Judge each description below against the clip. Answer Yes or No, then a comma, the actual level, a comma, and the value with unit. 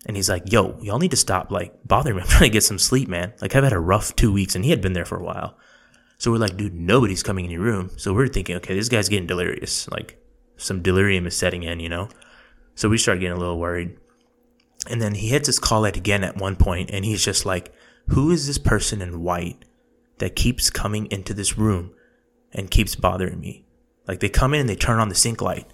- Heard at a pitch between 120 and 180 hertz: No, low, 100 Hz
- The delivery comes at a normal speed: No, fast, 250 wpm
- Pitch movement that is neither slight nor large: Yes, average, 3.9 semitones